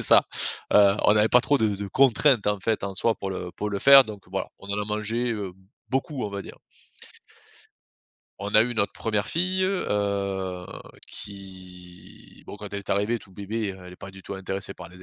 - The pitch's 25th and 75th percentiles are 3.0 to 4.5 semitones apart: No, narrow, 2.5 semitones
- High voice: No, low, 100 Hz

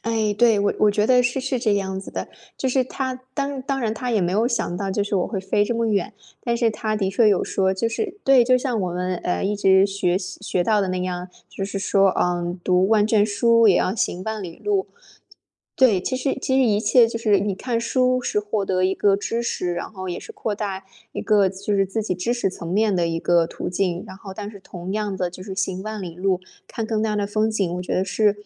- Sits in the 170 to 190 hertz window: No, high, 205 Hz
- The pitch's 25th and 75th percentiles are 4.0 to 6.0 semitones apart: No, average, 3.4 semitones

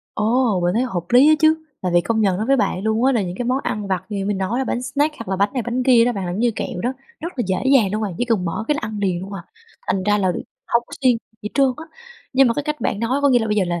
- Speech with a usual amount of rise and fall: Yes, average, 4.7 semitones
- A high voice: Yes, high, 220 Hz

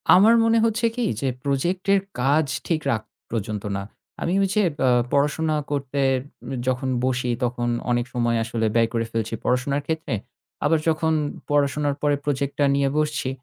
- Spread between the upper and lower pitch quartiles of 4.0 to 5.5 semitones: Yes, average, 4.4 semitones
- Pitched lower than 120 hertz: No, medium, 140 Hz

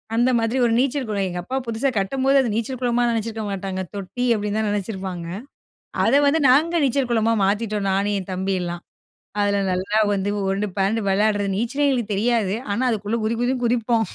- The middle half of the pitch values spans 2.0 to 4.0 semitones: Yes, average, 3.6 semitones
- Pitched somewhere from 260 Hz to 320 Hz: No, high, 220 Hz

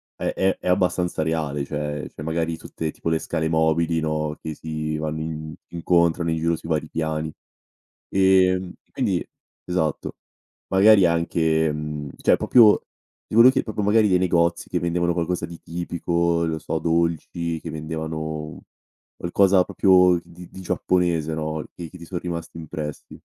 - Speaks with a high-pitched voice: No, very low, 85 Hz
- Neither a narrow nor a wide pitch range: No, narrow, 2.1 semitones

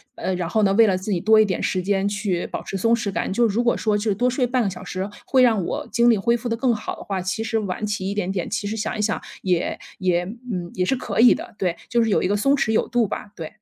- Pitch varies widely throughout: No, average, 3.4 semitones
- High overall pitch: Yes, high, 210 Hz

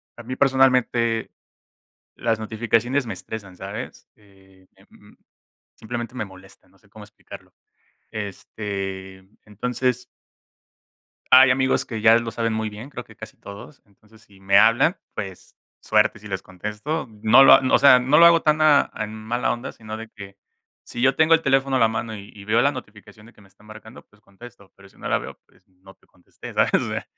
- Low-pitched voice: Yes, low, 110 Hz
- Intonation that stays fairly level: No, average, 3.8 semitones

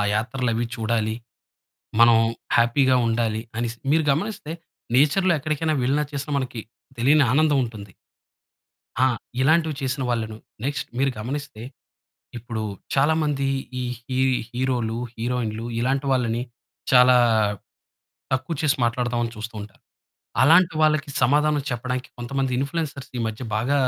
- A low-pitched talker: Yes, low, 130 Hz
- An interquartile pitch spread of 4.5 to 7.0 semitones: No, average, 3.7 semitones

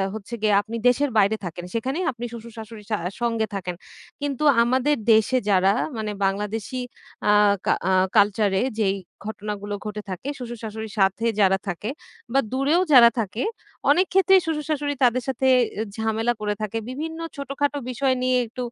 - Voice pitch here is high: Yes, high, 225 Hz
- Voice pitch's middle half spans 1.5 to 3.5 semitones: No, average, 4.0 semitones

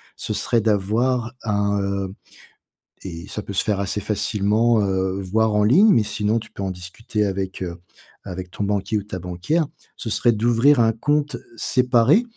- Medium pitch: No, low, 105 Hz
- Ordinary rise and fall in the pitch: Yes, average, 3.2 semitones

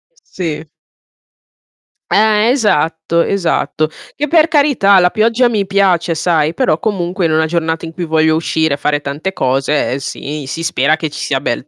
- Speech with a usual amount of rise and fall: Yes, average, 4.4 semitones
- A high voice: No, medium, 165 Hz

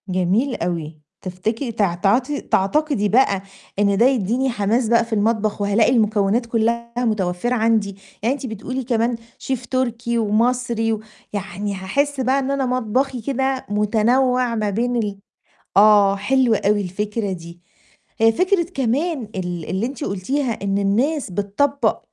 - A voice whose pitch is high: Yes, high, 225 Hz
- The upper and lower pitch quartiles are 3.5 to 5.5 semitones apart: Yes, average, 4.1 semitones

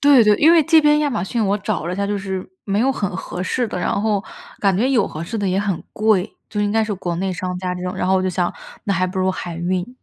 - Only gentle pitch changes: No, average, 3.2 semitones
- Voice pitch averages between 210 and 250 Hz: No, high, 195 Hz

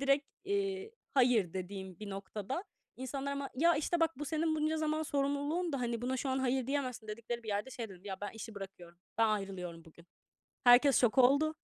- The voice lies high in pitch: Yes, very high, 255 Hz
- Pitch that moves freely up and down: Yes, wide, 6.0 semitones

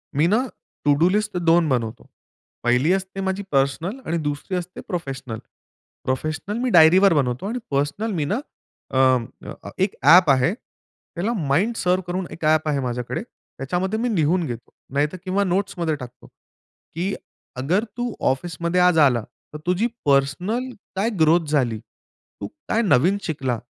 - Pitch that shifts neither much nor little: No, wide, 5.7 semitones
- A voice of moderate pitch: Yes, medium, 165 Hz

